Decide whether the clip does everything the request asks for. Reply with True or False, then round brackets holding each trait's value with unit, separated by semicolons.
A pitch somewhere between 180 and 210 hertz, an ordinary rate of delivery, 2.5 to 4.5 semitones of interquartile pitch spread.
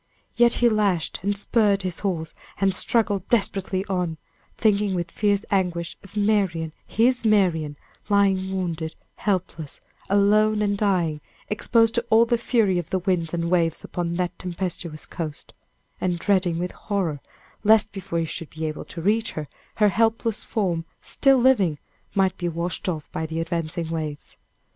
True (185 Hz; 160 wpm; 3.7 semitones)